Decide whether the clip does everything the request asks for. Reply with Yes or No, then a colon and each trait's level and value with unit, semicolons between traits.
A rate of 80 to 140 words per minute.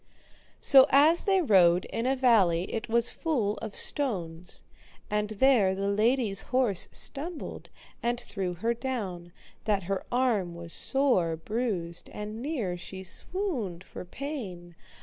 Yes: slow, 135 wpm